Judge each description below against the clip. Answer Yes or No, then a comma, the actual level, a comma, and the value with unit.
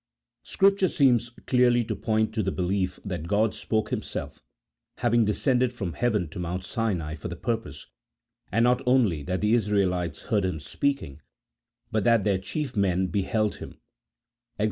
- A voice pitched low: Yes, low, 105 Hz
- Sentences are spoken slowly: No, average, 165 wpm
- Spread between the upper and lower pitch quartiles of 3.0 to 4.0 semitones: No, average, 4.7 semitones